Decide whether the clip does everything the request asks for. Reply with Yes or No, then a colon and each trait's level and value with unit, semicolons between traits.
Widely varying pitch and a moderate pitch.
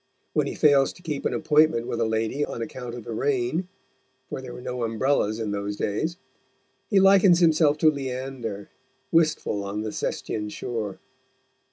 No: wide, 5.7 semitones; low, 125 Hz